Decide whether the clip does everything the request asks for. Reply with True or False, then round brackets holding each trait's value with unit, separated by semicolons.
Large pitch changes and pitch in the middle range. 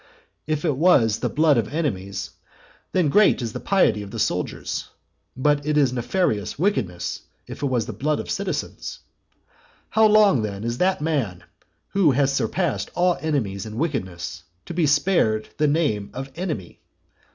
True (7.3 semitones; 145 Hz)